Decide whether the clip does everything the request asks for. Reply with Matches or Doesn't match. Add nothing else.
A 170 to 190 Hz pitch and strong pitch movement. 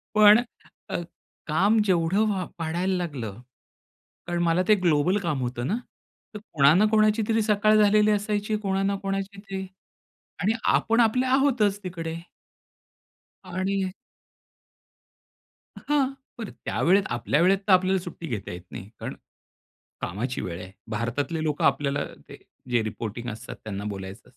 Matches